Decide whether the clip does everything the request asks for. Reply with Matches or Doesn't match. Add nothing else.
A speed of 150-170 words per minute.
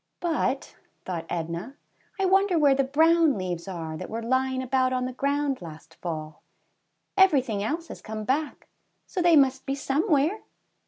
Matches